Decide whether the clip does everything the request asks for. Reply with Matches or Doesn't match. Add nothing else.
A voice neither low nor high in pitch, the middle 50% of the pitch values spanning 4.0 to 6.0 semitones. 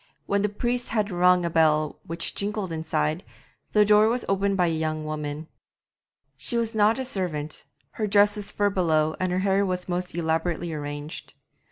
Matches